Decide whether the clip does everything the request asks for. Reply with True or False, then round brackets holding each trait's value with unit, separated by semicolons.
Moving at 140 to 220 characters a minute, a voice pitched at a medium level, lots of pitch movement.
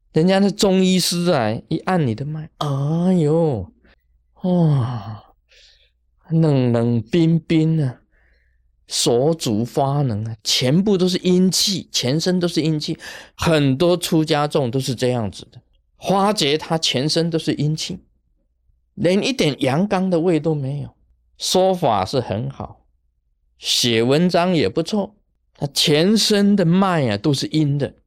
True (190 characters per minute; 150 Hz; 6.9 semitones)